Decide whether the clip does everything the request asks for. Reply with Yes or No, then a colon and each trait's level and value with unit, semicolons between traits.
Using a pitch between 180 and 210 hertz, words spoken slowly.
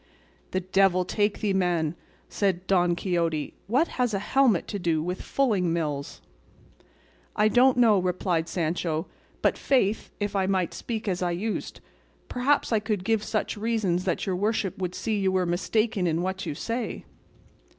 No: high, 190 Hz; average, 165 wpm